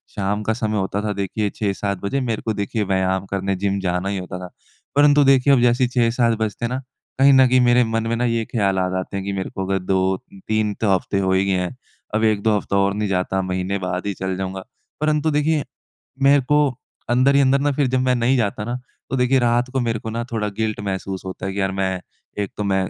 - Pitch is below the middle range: Yes, low, 105 Hz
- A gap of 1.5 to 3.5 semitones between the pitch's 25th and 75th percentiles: No, average, 4.3 semitones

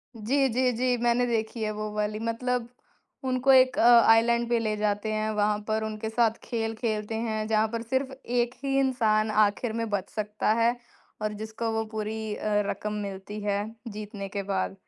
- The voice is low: No, high, 220 Hz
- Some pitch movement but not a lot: No, narrow, 1.9 semitones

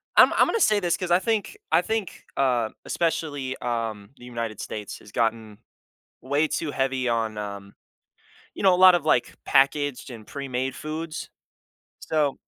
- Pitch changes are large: Yes, wide, 6.0 semitones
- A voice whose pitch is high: No, low, 135 Hz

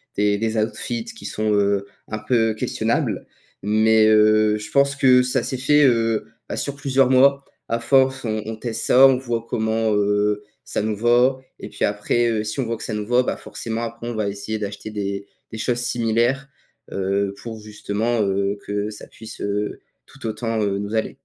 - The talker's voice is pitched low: Yes, low, 110 Hz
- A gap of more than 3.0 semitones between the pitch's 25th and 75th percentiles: No, average, 2.7 semitones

